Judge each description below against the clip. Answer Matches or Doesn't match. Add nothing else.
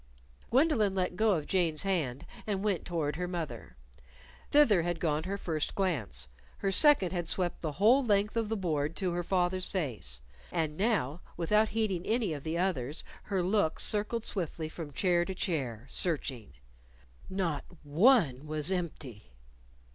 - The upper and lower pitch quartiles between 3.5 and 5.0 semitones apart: Matches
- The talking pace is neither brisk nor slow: Matches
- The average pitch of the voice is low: Doesn't match